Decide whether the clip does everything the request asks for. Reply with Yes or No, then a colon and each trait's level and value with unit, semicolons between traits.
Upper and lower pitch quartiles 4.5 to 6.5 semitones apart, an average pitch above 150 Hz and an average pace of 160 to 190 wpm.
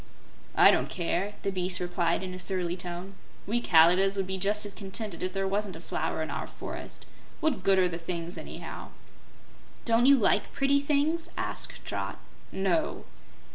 No: average, 2.9 semitones; high, 190 Hz; average, 175 wpm